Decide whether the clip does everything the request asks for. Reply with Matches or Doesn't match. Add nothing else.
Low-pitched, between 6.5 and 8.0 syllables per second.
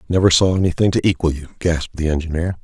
Matches